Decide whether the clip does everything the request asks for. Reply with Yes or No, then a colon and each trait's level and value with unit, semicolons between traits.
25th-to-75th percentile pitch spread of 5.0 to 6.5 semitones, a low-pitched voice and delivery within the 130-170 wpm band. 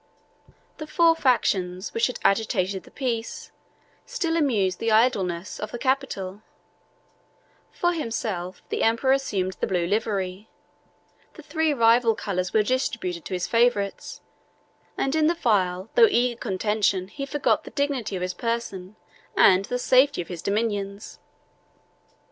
No: wide, 5.4 semitones; high, 220 Hz; average, 140 wpm